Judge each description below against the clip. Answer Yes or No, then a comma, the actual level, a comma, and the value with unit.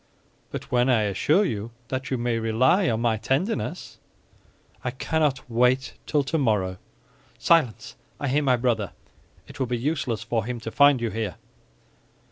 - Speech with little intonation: No, average, 3.9 semitones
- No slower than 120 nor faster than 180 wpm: Yes, average, 155 wpm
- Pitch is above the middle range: No, low, 125 Hz